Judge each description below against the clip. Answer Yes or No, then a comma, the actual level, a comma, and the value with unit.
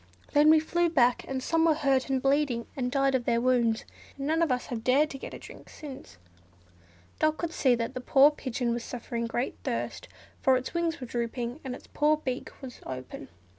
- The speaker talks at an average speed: No, fast, 215 wpm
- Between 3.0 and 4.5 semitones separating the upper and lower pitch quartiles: Yes, average, 3.6 semitones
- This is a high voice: Yes, very high, 260 Hz